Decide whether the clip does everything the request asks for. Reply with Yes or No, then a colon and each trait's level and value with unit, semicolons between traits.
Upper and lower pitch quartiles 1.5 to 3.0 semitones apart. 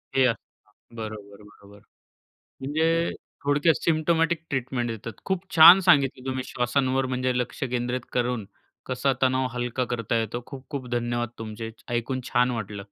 Yes: average, 2.7 semitones